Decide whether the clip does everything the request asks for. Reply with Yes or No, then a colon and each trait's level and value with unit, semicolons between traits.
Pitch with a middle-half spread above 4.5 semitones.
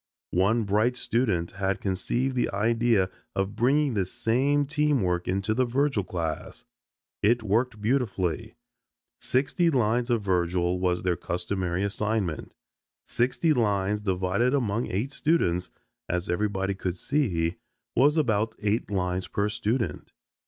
Yes: average, 4.9 semitones